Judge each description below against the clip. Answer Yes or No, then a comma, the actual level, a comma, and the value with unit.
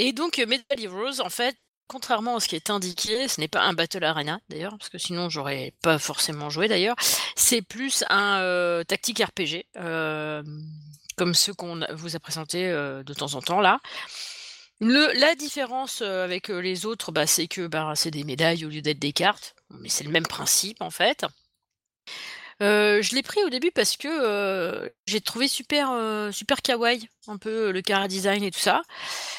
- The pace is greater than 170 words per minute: Yes, average, 190 wpm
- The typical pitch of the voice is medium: No, high, 195 Hz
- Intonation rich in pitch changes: Yes, wide, 6.6 semitones